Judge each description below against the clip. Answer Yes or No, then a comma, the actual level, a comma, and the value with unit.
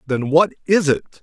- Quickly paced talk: No, average, 195 wpm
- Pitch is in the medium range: Yes, medium, 155 Hz